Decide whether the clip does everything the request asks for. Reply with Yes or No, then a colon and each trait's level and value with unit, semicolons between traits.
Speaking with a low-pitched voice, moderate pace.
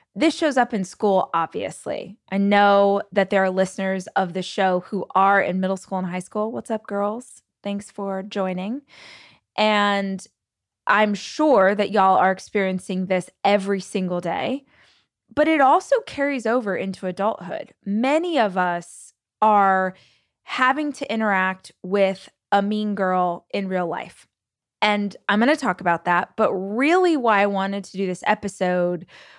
No: high, 200 Hz; average, 155 wpm